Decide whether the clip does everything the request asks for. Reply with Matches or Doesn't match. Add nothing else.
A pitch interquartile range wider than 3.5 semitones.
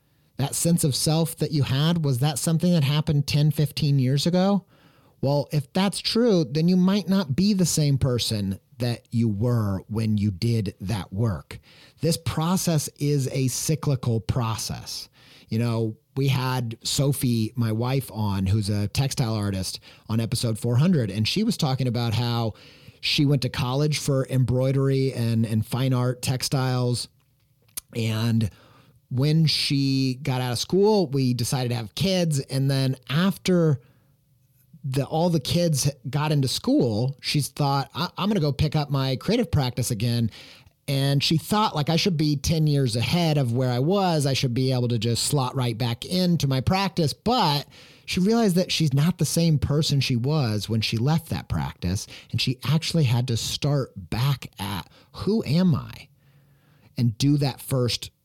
Matches